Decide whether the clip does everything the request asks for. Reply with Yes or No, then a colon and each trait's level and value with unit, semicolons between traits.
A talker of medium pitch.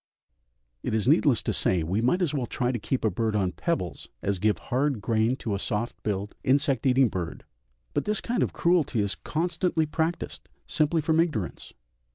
No: low, 125 Hz